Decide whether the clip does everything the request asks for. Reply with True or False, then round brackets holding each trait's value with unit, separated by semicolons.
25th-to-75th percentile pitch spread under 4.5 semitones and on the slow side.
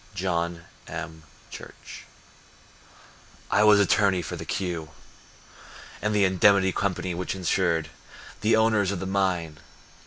True (2.8 semitones; 120 wpm)